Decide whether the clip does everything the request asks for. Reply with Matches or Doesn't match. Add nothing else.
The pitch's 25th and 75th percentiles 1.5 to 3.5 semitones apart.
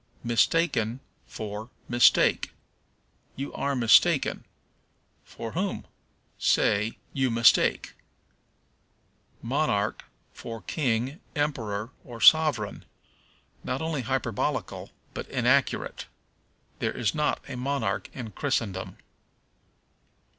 Doesn't match